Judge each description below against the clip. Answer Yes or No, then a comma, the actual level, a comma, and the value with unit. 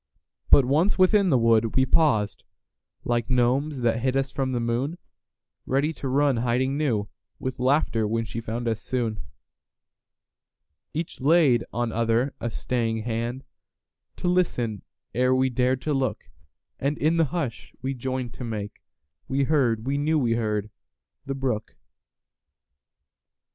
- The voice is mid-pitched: No, low, 125 Hz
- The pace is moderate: No, slow, 125 wpm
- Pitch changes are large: No, average, 3.3 semitones